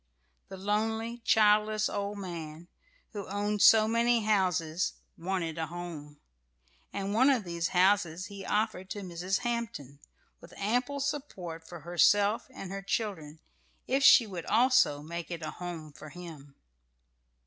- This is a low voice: No, high, 195 Hz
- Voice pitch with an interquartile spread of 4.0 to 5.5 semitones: Yes, average, 4.3 semitones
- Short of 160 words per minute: Yes, average, 140 wpm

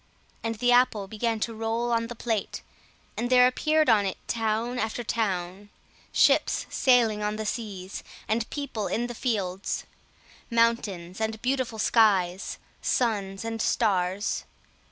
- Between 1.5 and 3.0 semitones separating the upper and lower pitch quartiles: Yes, average, 2.7 semitones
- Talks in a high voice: Yes, high, 225 Hz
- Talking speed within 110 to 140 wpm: Yes, slow, 135 wpm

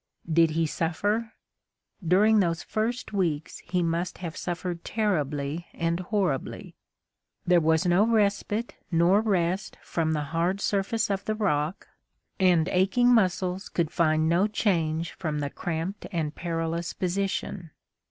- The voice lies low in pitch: No, medium, 175 Hz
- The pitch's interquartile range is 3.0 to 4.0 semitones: Yes, average, 3.4 semitones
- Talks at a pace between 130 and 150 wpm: Yes, slow, 135 wpm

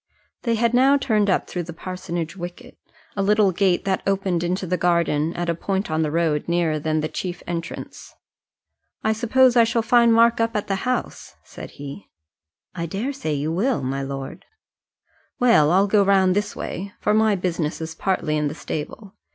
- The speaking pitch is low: No, medium, 185 Hz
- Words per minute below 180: No, average, 185 wpm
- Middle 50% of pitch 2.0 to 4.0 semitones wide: No, average, 4.5 semitones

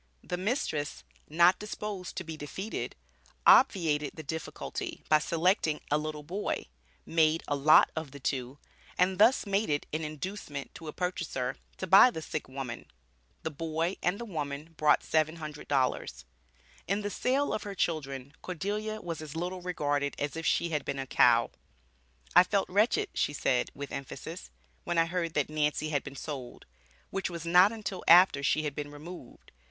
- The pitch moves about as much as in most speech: Yes, average, 4.0 semitones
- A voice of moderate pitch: Yes, medium, 160 Hz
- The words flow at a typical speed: Yes, average, 170 wpm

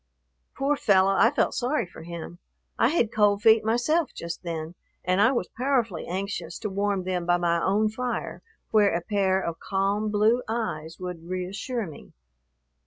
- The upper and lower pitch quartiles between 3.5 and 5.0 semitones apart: Yes, average, 4.1 semitones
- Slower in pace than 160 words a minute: No, average, 170 wpm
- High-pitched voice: Yes, high, 200 Hz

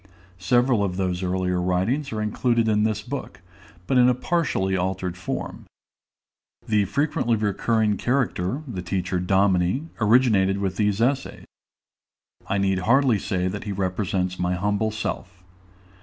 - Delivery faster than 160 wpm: No, average, 140 wpm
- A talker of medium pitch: No, low, 100 Hz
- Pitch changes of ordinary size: Yes, average, 4.1 semitones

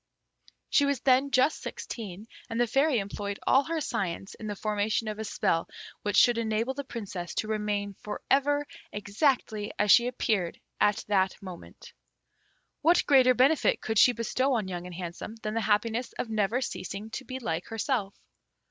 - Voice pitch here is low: No, high, 220 Hz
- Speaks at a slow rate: No, average, 175 wpm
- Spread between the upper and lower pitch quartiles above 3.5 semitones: Yes, average, 4.1 semitones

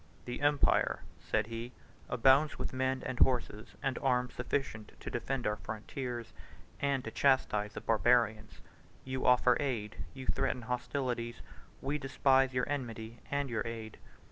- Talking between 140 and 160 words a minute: Yes, average, 145 wpm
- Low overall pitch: Yes, low, 125 Hz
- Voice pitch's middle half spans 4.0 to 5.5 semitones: No, average, 2.7 semitones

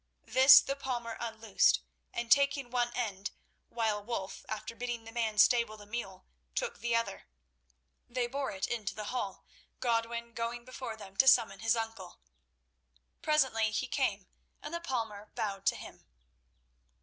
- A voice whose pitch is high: Yes, high, 230 Hz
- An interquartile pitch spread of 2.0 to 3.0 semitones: Yes, narrow, 2.5 semitones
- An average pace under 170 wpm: Yes, average, 150 wpm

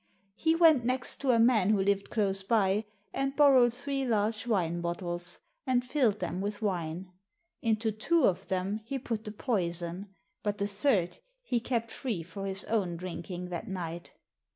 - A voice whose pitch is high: Yes, high, 205 Hz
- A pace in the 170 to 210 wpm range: Yes, average, 175 wpm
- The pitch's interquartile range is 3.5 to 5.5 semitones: Yes, average, 4.8 semitones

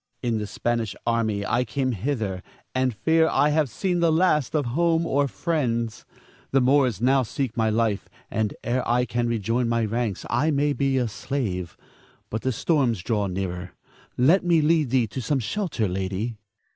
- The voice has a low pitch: Yes, low, 120 Hz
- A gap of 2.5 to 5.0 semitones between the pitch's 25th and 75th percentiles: Yes, average, 4.5 semitones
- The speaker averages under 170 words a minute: No, average, 175 wpm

